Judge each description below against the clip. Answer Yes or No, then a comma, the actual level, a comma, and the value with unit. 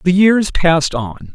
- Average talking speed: Yes, average, 180 wpm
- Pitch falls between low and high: Yes, medium, 170 Hz